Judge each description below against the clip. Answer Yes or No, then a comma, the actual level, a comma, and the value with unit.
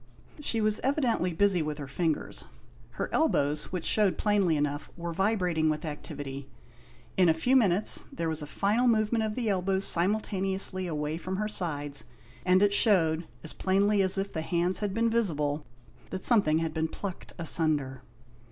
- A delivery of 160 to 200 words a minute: Yes, average, 170 wpm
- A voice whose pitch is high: No, medium, 180 Hz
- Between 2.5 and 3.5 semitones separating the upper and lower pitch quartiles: No, average, 4.6 semitones